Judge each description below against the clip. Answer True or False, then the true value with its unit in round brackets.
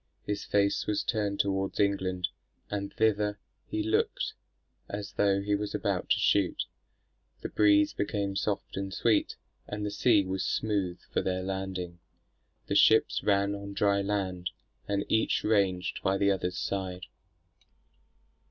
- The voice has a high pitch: False (100 Hz)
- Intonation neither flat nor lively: False (1.4 semitones)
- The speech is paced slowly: False (145 wpm)